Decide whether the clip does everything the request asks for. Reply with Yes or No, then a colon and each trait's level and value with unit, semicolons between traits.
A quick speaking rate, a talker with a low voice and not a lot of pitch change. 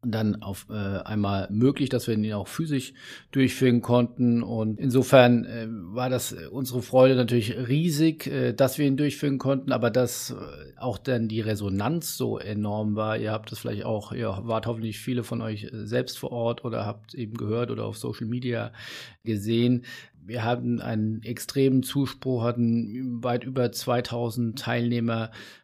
No: average, 155 wpm; low, 120 Hz; narrow, 2.3 semitones